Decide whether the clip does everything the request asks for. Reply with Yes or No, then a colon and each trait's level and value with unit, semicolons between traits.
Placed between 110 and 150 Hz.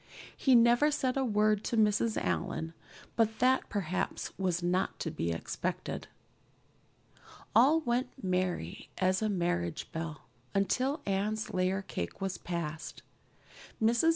No: high, 195 Hz